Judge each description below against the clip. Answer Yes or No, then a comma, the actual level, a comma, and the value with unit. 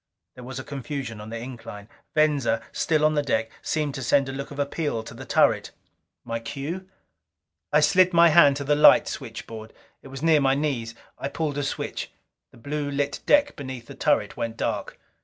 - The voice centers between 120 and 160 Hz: Yes, medium, 140 Hz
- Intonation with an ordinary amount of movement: Yes, average, 4.1 semitones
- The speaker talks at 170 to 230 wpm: Yes, average, 195 wpm